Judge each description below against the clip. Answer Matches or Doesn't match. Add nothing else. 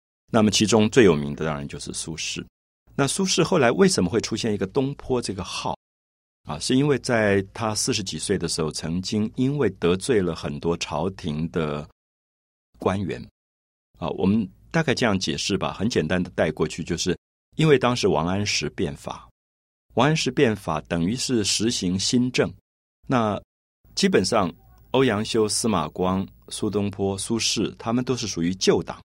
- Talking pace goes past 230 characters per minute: Matches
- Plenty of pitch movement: Matches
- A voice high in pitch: Doesn't match